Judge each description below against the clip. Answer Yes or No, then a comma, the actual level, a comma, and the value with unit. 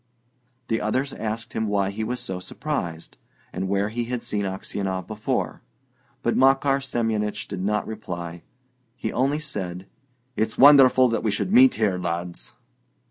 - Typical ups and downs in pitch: Yes, average, 5.0 semitones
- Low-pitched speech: Yes, low, 110 Hz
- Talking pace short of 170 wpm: Yes, average, 150 wpm